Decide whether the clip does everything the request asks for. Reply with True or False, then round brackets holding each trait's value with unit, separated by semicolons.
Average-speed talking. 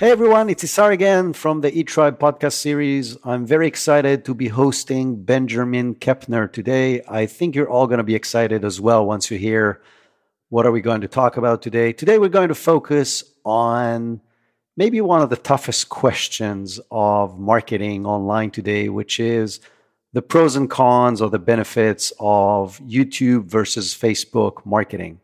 True (170 wpm)